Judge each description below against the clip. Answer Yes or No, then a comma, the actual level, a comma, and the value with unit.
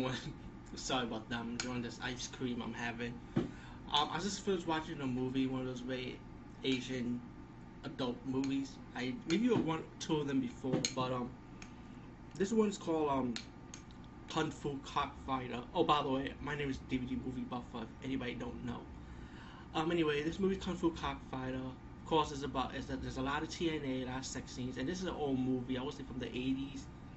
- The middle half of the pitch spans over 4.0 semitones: No, average, 3.3 semitones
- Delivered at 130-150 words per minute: No, average, 200 wpm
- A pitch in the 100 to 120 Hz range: No, low, 130 Hz